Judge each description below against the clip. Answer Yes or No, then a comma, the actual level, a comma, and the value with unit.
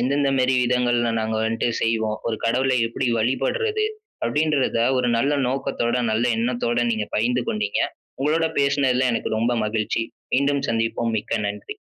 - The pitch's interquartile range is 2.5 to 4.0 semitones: Yes, average, 3.0 semitones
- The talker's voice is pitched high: No, low, 120 Hz